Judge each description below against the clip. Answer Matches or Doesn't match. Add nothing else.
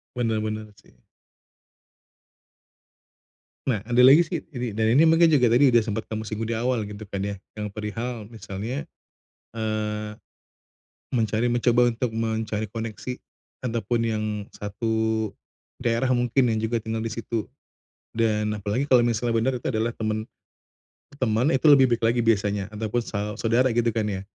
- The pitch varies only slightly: Matches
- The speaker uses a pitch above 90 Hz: Matches